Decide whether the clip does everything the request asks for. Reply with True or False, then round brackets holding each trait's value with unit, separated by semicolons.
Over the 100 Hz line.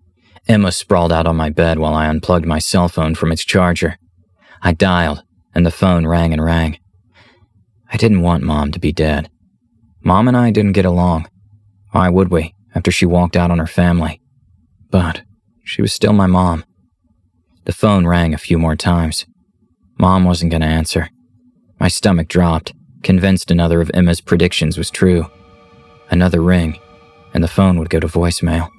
False (90 Hz)